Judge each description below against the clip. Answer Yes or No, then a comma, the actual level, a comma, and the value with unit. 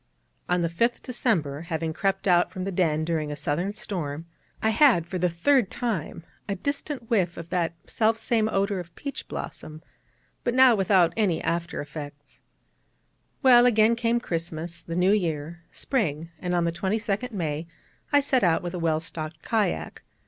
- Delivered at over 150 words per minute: Yes, average, 170 wpm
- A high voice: No, medium, 180 Hz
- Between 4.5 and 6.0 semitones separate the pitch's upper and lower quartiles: Yes, average, 5.2 semitones